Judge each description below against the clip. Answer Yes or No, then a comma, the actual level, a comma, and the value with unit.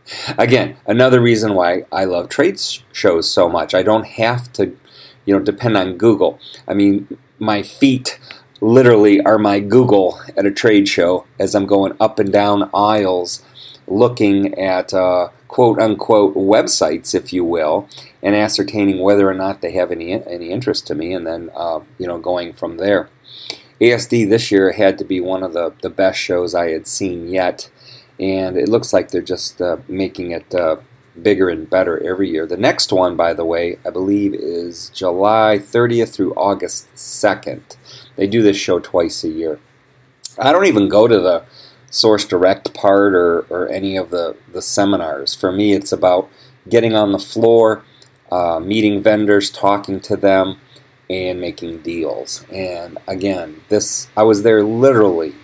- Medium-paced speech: Yes, average, 170 wpm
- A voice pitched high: No, low, 100 Hz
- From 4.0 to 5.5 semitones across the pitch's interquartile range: No, average, 2.9 semitones